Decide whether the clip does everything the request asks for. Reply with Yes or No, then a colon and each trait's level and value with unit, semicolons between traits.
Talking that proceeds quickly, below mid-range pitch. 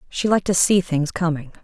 No: fast, 220 wpm; medium, 170 Hz